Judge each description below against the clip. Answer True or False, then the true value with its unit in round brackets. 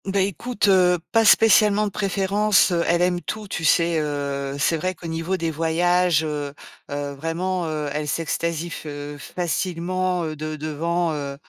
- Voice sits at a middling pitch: True (170 Hz)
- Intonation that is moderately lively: True (3.3 semitones)